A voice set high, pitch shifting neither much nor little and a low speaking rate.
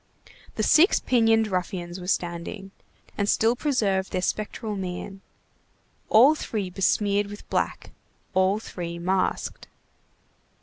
Yes: high, 195 Hz; average, 3.2 semitones; slow, 115 wpm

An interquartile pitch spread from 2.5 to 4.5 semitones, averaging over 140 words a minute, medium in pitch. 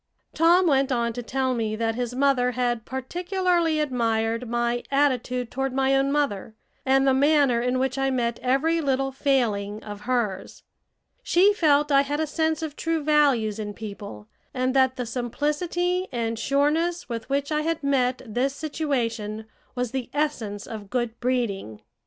No: average, 3.9 semitones; average, 165 wpm; very high, 260 Hz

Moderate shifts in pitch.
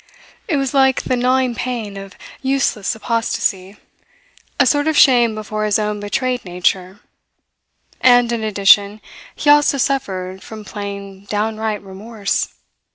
Yes: average, 4.1 semitones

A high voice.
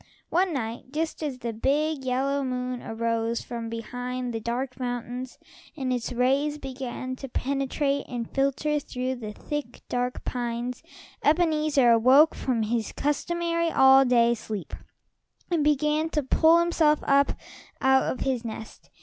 Yes: very high, 260 Hz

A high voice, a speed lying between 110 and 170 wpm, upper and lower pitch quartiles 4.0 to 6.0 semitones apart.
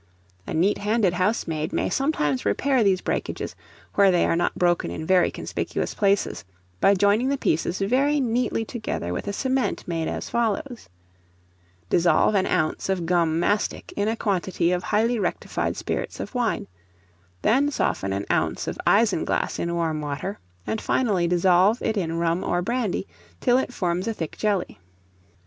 Yes: high, 195 Hz; average, 165 wpm; average, 4.9 semitones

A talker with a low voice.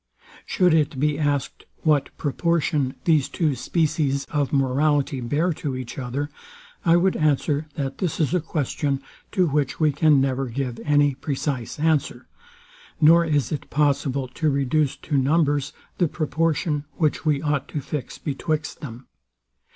No: medium, 145 Hz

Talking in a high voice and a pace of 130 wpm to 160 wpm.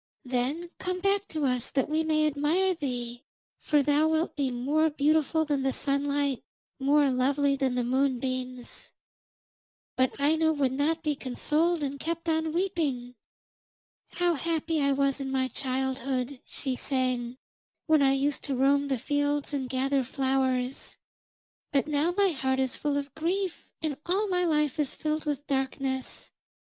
Yes: very high, 280 Hz; average, 155 wpm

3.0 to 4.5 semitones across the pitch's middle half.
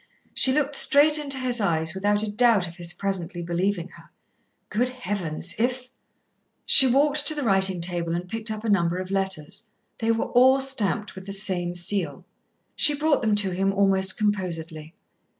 No: wide, 5.6 semitones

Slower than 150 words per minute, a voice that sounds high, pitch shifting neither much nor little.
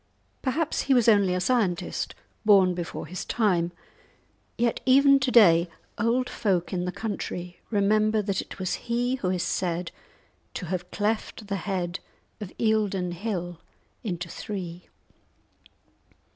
Yes: slow, 135 wpm; high, 200 Hz; average, 4.0 semitones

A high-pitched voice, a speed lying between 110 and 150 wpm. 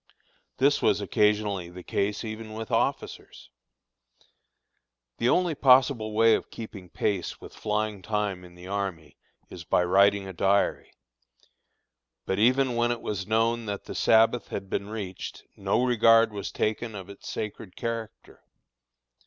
No: low, 105 Hz; average, 145 wpm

